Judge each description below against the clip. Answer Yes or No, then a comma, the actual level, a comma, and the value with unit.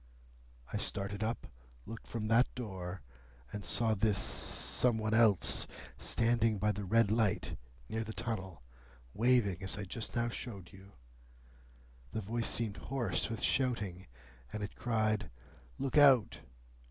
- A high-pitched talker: No, low, 110 Hz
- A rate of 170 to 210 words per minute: No, average, 140 wpm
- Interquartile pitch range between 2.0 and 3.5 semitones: Yes, average, 2.8 semitones